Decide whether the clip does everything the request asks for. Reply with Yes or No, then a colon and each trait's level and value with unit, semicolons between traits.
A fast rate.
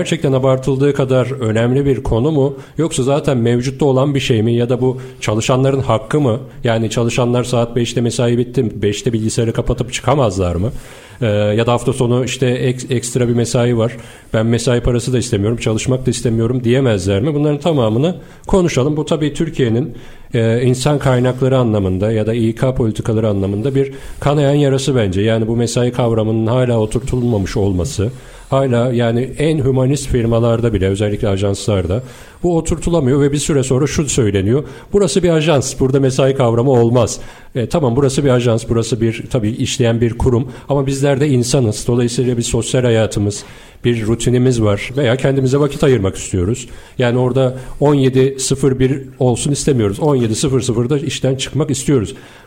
Yes: fast, 155 wpm